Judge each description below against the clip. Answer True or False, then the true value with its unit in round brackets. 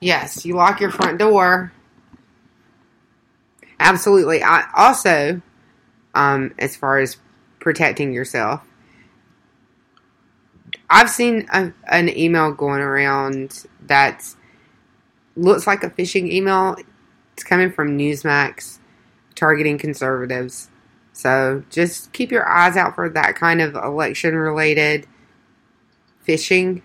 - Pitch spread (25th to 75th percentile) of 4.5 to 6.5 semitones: True (5.3 semitones)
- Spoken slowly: True (105 wpm)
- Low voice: False (150 Hz)